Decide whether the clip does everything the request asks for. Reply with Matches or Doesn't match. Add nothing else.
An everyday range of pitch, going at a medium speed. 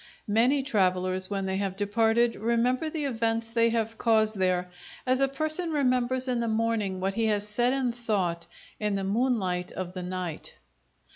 Matches